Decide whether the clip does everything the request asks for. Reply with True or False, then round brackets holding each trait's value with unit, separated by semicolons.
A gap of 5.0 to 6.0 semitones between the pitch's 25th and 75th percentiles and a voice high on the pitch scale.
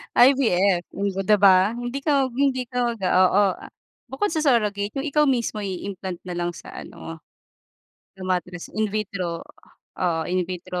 True (5.3 semitones; 200 Hz)